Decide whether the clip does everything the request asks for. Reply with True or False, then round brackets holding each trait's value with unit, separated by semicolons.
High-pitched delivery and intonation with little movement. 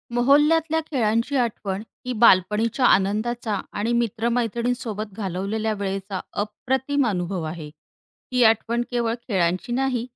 False (225 Hz; 3.6 semitones)